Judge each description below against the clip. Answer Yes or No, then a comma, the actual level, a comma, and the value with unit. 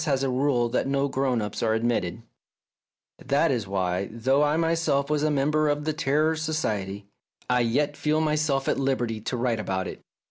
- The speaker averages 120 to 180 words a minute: No, average, 190 wpm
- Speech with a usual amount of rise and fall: Yes, average, 4.7 semitones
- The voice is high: No, low, 135 Hz